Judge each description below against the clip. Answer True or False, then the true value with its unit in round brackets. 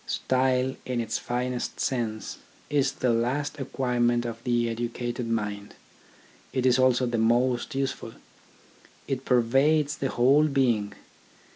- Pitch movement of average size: False (2.0 semitones)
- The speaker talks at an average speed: False (125 wpm)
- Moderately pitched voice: False (125 Hz)